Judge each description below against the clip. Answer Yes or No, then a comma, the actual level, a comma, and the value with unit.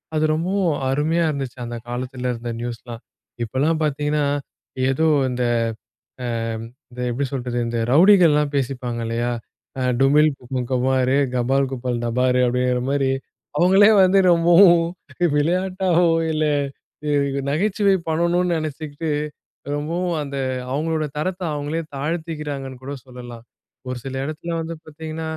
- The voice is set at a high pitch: No, medium, 145 Hz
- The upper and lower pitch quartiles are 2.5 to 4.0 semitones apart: No, average, 4.5 semitones